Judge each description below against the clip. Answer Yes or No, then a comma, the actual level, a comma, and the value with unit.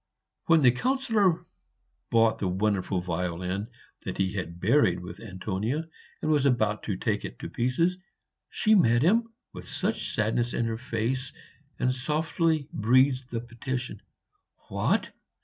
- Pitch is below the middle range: Yes, low, 120 Hz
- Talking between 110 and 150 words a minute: Yes, average, 140 wpm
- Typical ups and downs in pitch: No, wide, 6.4 semitones